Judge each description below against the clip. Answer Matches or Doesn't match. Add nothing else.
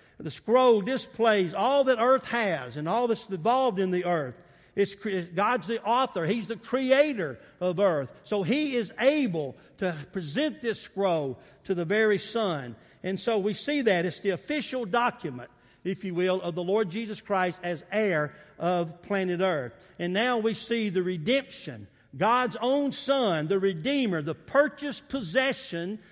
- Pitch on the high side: Matches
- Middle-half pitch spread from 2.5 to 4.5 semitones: Doesn't match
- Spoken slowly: Doesn't match